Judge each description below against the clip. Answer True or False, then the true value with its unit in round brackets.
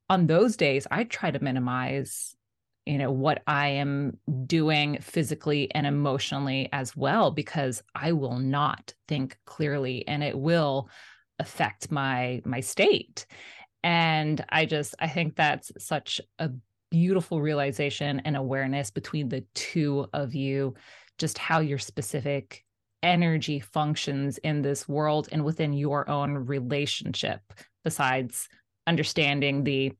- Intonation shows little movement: True (2.2 semitones)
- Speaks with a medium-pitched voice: True (145 Hz)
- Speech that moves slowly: True (130 wpm)